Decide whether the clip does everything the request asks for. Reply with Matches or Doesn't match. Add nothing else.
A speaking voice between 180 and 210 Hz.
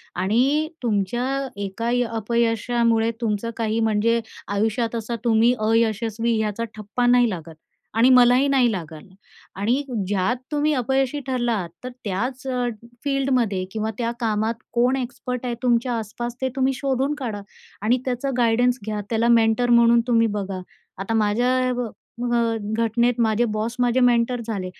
Doesn't match